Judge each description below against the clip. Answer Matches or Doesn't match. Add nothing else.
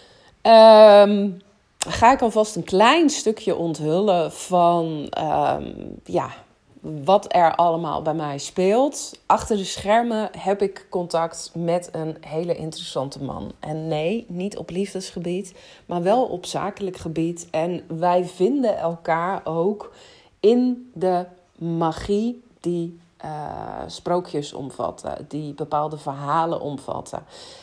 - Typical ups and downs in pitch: Matches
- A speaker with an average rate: Doesn't match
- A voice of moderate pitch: Matches